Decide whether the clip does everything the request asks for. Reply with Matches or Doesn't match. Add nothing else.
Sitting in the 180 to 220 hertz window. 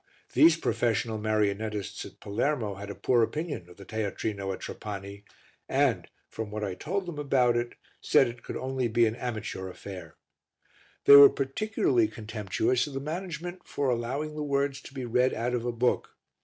Doesn't match